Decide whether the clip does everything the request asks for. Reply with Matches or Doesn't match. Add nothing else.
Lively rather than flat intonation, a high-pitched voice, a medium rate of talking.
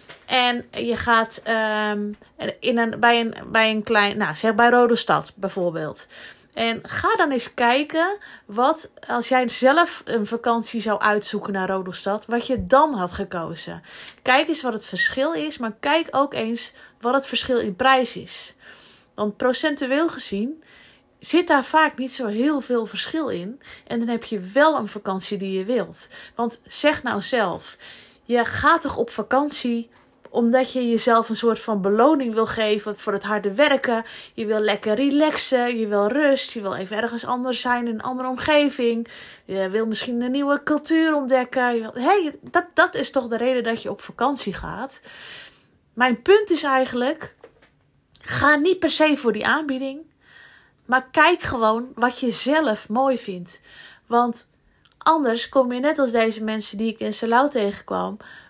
Doesn't match